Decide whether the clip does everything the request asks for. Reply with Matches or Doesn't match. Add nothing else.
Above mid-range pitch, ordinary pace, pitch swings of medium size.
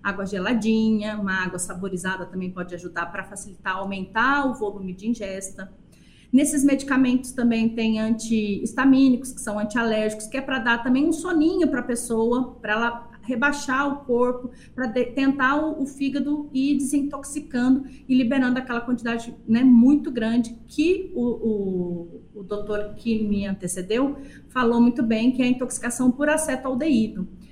Matches